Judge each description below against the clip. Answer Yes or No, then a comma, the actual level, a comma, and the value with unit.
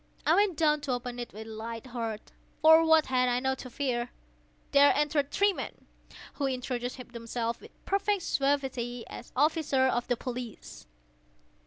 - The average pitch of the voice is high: Yes, very high, 255 Hz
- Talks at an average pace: Yes, average, 160 wpm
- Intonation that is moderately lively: Yes, average, 3.5 semitones